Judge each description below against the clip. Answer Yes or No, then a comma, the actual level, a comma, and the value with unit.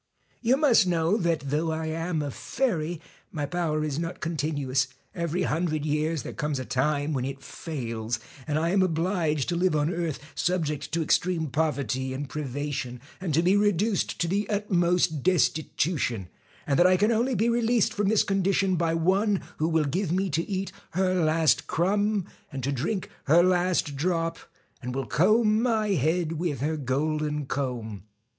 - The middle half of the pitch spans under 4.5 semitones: Yes, average, 4.1 semitones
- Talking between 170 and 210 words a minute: Yes, average, 175 wpm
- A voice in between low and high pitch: Yes, medium, 165 Hz